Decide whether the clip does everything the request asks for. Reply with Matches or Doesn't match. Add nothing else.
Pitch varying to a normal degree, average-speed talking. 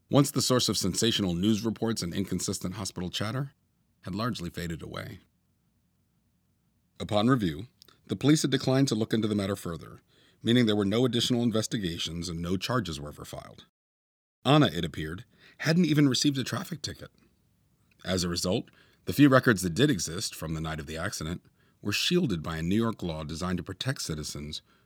Doesn't match